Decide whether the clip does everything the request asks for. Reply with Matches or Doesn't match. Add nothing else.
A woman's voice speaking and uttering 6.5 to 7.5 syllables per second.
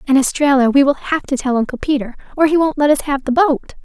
Matches